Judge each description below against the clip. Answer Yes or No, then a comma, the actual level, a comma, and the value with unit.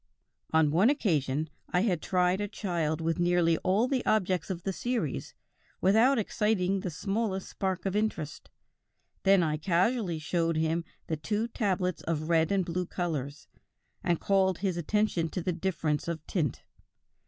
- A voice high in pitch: No, medium, 180 Hz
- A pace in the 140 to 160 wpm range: Yes, average, 155 wpm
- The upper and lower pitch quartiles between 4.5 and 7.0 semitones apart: No, average, 3.3 semitones